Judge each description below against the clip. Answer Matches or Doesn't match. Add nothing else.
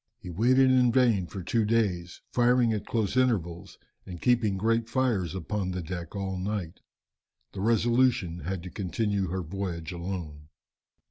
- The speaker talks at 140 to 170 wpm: Matches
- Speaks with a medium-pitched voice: Doesn't match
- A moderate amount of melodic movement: Matches